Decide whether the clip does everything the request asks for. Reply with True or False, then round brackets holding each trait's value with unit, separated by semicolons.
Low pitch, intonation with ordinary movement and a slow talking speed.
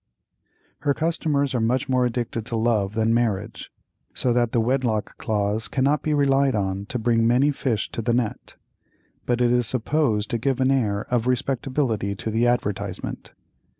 False (120 Hz; 3.0 semitones; 170 wpm)